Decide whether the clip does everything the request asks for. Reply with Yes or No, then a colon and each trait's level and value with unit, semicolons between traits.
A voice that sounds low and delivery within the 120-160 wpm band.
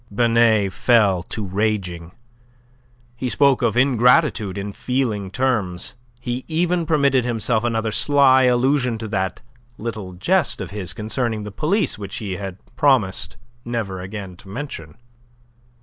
Yes: low, 115 Hz; slow, 135 wpm